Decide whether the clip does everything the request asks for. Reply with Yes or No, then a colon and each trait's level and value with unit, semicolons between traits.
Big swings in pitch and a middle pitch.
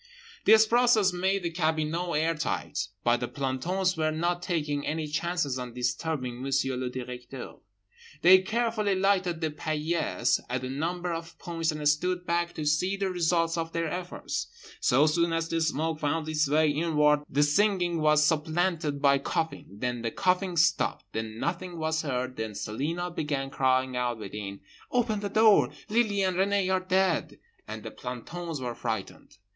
No: average, 4.8 semitones; medium, 160 Hz